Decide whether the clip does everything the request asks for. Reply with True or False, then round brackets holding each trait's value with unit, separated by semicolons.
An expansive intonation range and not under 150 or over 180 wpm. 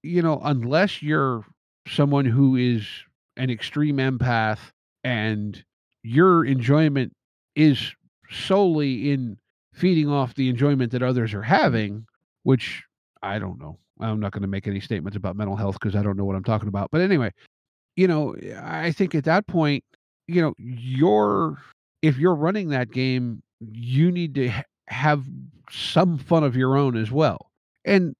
True (5.8 semitones; 160 wpm)